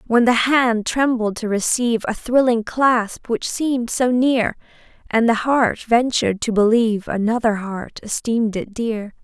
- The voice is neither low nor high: No, high, 230 Hz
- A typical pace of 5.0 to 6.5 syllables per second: No, 4.4 syllables/s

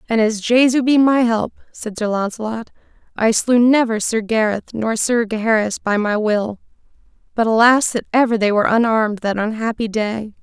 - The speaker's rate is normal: Yes, average, 175 wpm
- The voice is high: Yes, high, 225 Hz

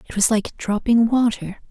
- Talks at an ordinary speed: Yes, average, 175 wpm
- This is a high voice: Yes, high, 220 Hz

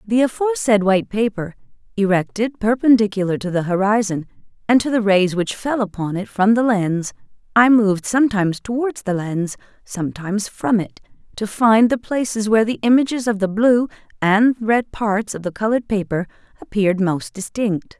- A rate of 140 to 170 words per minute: Yes, average, 165 wpm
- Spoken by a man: No, female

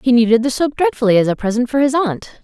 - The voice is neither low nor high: No, very high, 250 Hz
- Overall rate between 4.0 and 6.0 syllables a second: No, 6.4 syllables/s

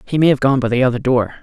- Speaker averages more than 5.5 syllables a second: Yes, 7.3 syllables/s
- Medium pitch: No, low, 130 Hz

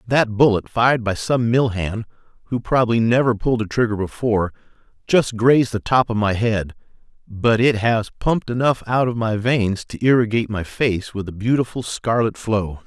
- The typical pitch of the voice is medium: No, low, 115 Hz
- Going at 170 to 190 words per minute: Yes, average, 180 wpm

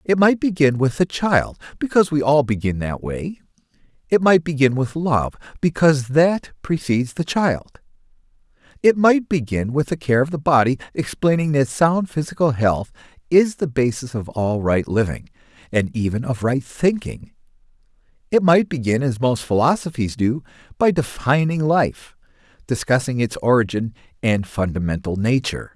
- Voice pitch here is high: No, medium, 140 Hz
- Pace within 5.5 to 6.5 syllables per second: No, 4.8 syllables/s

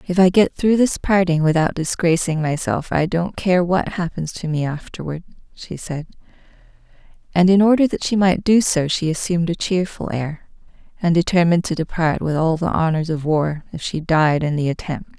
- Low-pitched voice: No, medium, 170 Hz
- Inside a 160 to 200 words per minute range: Yes, average, 190 wpm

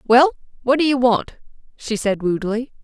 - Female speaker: Yes, female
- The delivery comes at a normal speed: Yes, average, 170 wpm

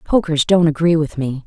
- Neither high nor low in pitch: Yes, medium, 160 Hz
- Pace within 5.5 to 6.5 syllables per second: No, 5.1 syllables/s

